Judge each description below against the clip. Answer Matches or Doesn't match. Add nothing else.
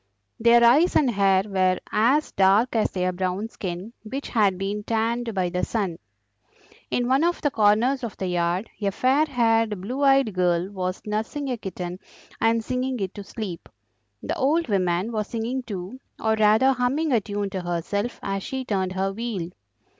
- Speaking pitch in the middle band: Doesn't match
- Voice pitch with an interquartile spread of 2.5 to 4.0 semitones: Doesn't match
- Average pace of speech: Matches